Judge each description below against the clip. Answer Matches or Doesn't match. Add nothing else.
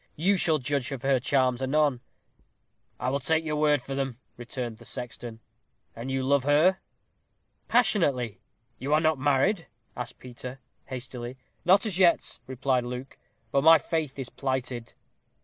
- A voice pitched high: Doesn't match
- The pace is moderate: Matches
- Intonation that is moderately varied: Matches